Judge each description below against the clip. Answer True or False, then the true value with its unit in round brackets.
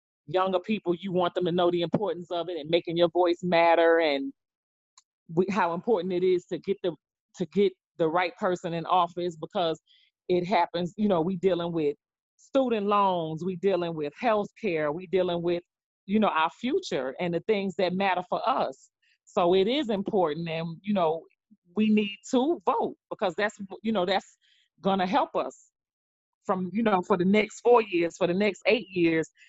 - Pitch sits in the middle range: True (180 Hz)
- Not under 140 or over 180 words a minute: False (190 wpm)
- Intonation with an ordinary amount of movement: True (3.2 semitones)